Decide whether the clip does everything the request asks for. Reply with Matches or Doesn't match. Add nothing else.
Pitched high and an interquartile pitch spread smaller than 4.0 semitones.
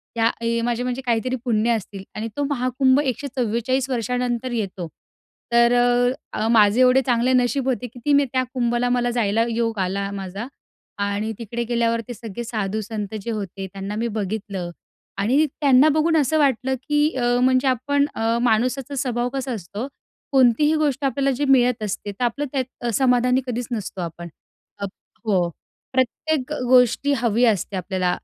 Matches